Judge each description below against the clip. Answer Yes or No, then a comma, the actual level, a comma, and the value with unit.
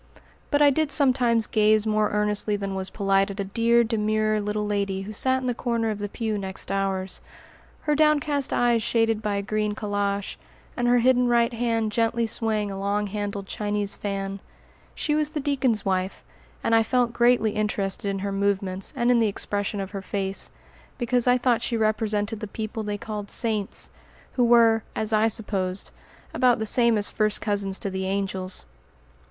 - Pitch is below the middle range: No, high, 215 Hz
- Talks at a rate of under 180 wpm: No, average, 185 wpm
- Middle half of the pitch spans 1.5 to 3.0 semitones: Yes, average, 2.7 semitones